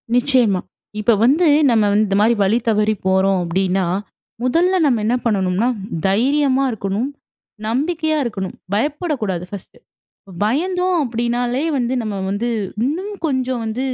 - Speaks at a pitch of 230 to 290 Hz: Yes, high, 235 Hz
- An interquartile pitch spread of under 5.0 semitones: No, average, 5.3 semitones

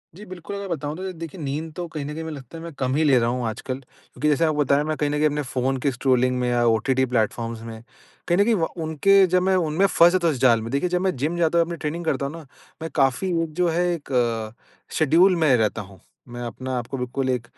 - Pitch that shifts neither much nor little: Yes, average, 5.0 semitones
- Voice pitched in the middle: Yes, medium, 145 Hz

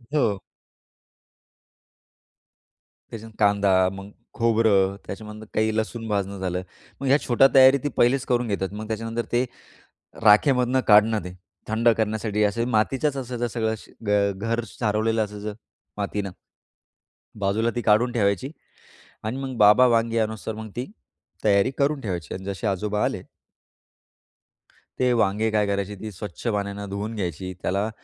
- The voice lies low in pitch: Yes, low, 110 Hz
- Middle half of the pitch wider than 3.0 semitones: No, narrow, 2.5 semitones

